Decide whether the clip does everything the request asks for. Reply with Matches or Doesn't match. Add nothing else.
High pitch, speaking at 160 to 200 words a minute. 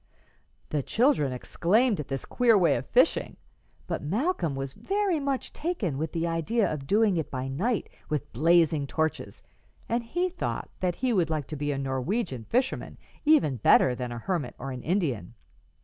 Doesn't match